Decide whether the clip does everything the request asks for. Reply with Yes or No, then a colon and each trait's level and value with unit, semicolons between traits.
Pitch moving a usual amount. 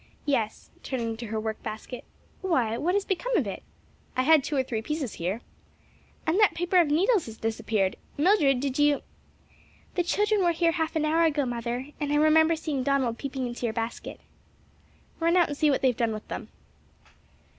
No: wide, 5.7 semitones